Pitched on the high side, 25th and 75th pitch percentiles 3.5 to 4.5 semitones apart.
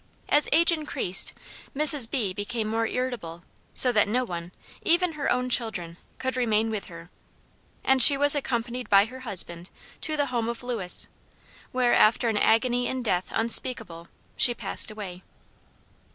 Yes: high, 235 Hz; average, 4.0 semitones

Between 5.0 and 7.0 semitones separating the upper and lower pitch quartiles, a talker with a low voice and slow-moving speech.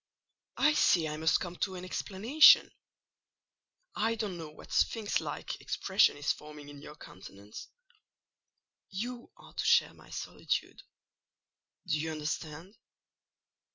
No: wide, 5.6 semitones; medium, 170 Hz; slow, 125 wpm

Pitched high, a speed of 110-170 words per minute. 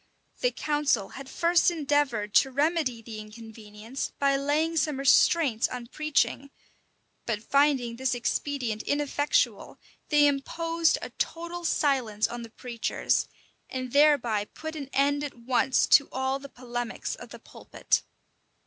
Yes: very high, 275 Hz; slow, 135 wpm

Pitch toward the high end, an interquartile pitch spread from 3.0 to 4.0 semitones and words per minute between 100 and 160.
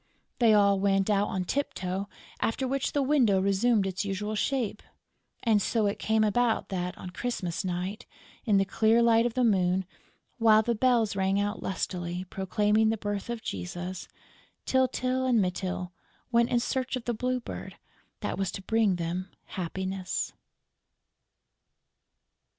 Yes: high, 205 Hz; average, 3.7 semitones; average, 155 wpm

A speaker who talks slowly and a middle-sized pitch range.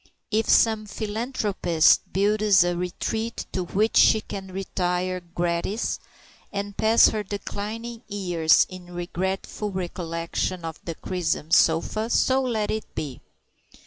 Yes: slow, 120 wpm; average, 3.5 semitones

